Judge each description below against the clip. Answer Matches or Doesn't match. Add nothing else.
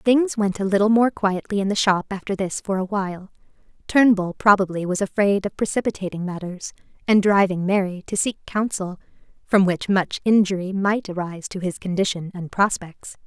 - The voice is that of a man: Doesn't match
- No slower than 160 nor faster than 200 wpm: Matches